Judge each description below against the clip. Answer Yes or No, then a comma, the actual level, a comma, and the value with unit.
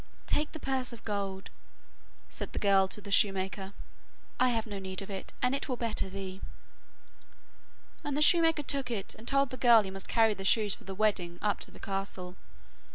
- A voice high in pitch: Yes, high, 210 Hz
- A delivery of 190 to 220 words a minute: Yes, average, 200 wpm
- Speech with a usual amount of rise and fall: Yes, average, 4.5 semitones